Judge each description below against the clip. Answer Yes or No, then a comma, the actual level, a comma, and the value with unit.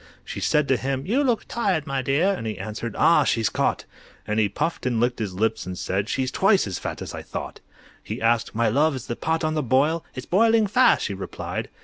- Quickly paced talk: Yes, fast, 235 wpm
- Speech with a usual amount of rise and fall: No, wide, 6.6 semitones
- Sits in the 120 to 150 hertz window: Yes, low, 135 Hz